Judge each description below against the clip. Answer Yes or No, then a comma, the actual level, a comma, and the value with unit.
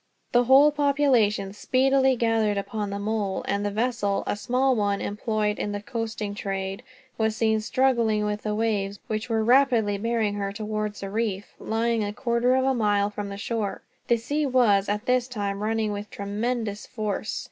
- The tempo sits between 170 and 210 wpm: Yes, average, 180 wpm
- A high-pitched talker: Yes, high, 215 Hz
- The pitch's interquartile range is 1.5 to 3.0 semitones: Yes, average, 2.7 semitones